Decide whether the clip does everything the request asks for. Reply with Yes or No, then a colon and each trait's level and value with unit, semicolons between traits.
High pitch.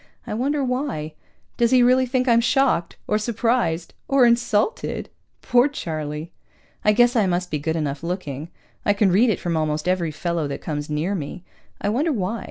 Yes: high, 200 Hz